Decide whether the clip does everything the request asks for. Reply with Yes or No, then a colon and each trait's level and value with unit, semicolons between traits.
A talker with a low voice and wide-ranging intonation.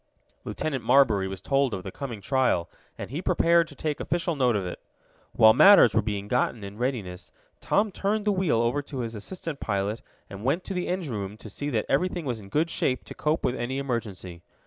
Yes: low, 125 Hz; wide, 7.0 semitones